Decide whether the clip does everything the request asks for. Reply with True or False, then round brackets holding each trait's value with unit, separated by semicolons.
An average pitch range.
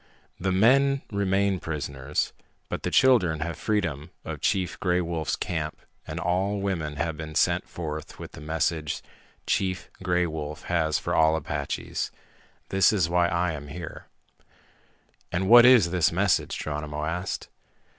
True (3.6 semitones)